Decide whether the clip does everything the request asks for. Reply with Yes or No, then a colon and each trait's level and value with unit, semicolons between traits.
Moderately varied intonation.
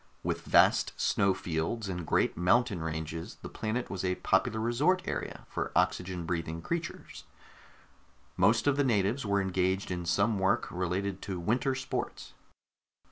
Yes: average, 4.8 semitones